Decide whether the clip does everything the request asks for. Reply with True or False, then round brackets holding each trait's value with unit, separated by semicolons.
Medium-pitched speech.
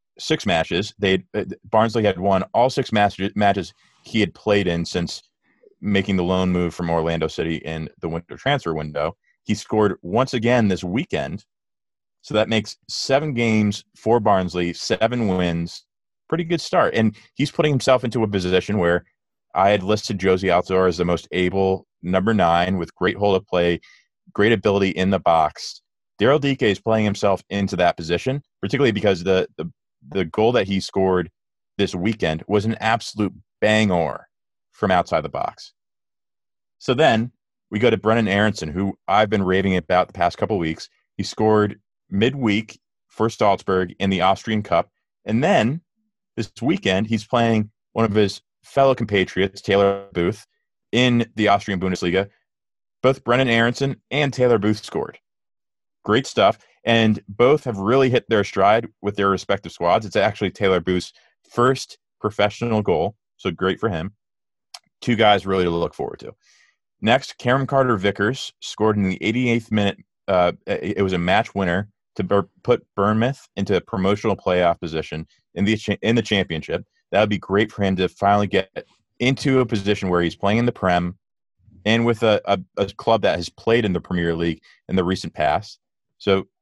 False (100 Hz)